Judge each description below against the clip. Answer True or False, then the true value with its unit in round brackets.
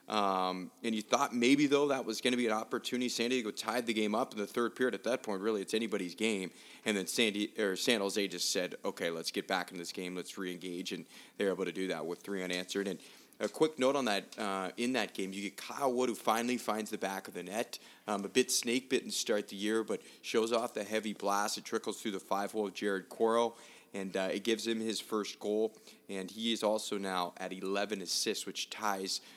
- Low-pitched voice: True (105 Hz)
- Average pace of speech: False (245 wpm)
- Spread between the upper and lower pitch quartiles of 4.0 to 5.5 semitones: False (3.2 semitones)